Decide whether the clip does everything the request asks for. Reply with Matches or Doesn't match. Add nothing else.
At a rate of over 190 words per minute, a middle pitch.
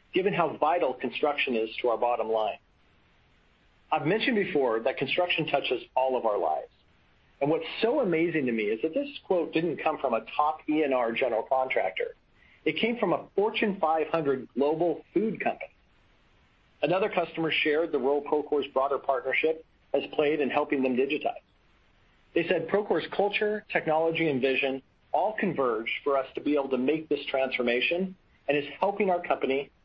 Doesn't match